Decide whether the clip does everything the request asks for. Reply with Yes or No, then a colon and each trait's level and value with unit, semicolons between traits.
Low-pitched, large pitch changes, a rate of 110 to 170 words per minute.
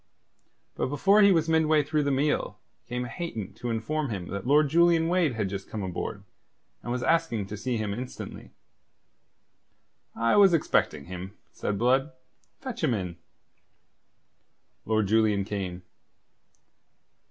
Yes: low, 125 Hz; wide, 7.3 semitones; average, 140 wpm